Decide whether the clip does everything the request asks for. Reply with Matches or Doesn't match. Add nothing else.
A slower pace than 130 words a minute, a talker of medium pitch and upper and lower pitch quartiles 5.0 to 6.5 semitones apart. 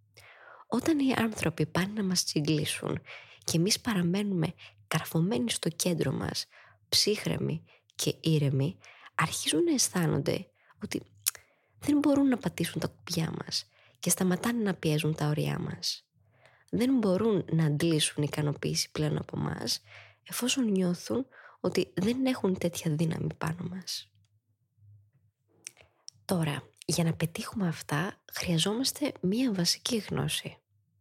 Matches